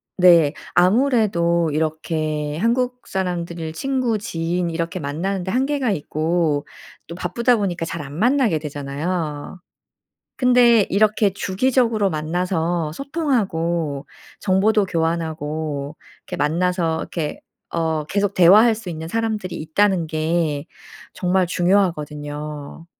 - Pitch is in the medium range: Yes, medium, 175 Hz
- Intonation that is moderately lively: Yes, average, 4.6 semitones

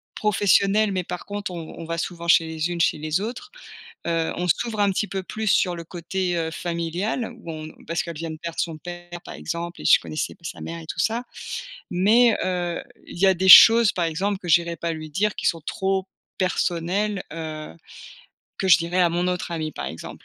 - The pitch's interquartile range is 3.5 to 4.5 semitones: No, average, 2.7 semitones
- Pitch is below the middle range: No, medium, 175 Hz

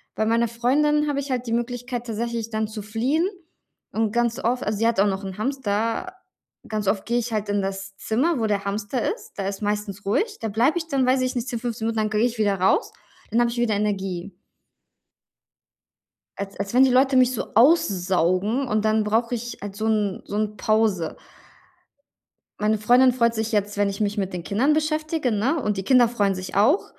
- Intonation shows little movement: No, average, 3.3 semitones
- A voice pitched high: Yes, high, 220 Hz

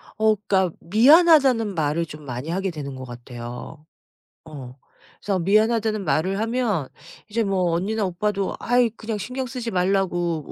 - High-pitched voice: Yes, high, 195 Hz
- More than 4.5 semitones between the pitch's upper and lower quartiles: Yes, wide, 5.6 semitones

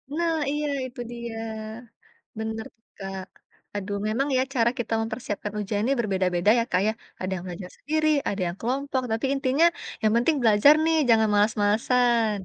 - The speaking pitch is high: Yes, high, 225 Hz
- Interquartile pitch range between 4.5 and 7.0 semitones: No, average, 3.9 semitones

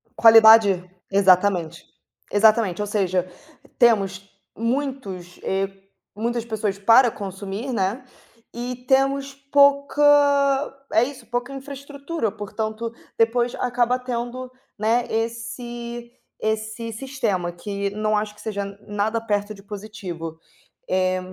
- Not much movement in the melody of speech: No, average, 3.7 semitones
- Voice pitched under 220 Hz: No, high, 225 Hz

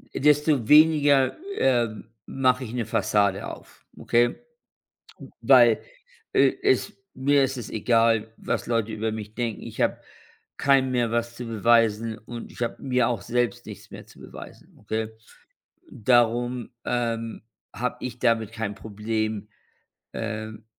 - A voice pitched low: Yes, low, 115 Hz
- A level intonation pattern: Yes, narrow, 2.2 semitones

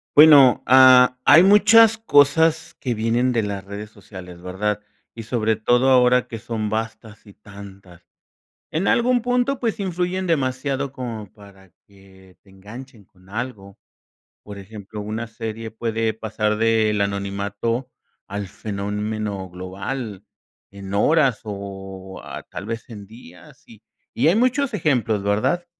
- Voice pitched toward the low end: Yes, low, 110 Hz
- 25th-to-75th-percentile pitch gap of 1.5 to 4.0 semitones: No, average, 4.5 semitones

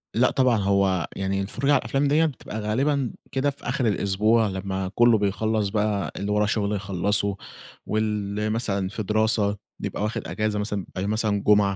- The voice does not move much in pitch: Yes, narrow, 2.0 semitones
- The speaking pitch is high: No, low, 105 Hz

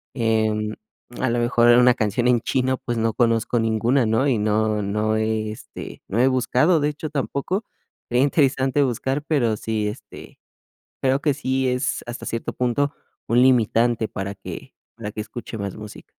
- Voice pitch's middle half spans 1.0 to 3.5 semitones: Yes, average, 3.2 semitones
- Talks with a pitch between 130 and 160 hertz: No, low, 120 Hz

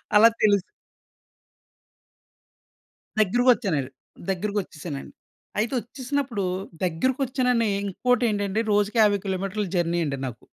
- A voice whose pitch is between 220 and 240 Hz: No, high, 205 Hz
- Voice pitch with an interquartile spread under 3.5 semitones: No, average, 4.9 semitones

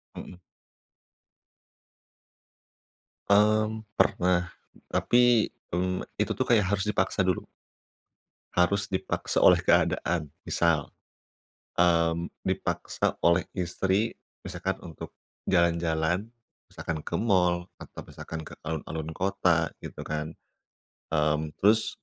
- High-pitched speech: No, very low, 90 Hz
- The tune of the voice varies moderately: Yes, average, 3.2 semitones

